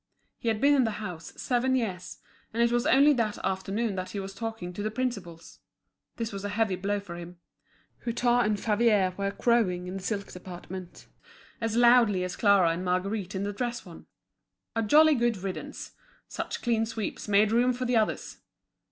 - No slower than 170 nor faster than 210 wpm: Yes, average, 185 wpm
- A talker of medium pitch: No, high, 210 Hz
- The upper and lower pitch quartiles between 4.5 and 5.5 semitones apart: No, average, 3.8 semitones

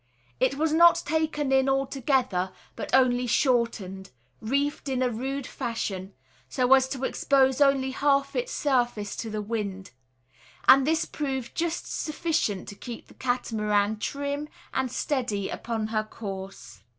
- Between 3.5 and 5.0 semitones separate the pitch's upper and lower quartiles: Yes, average, 4.4 semitones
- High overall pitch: Yes, very high, 260 Hz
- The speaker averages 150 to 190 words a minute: No, average, 140 wpm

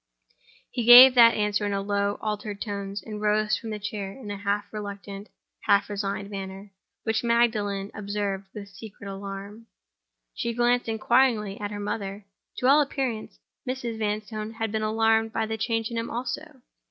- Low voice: No, high, 215 Hz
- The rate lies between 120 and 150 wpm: No, average, 165 wpm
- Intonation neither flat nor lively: No, narrow, 2.0 semitones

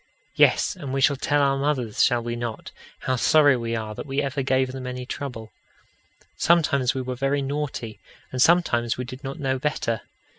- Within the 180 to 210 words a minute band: Yes, average, 190 wpm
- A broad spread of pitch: No, average, 2.8 semitones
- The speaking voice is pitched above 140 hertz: No, low, 130 Hz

